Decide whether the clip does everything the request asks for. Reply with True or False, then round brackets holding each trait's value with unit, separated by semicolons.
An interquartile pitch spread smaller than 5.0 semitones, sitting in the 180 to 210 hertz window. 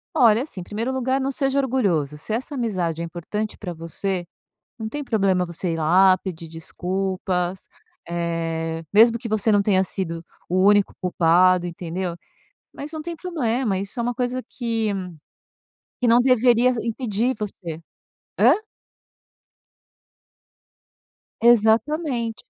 False (5.4 semitones; 205 Hz)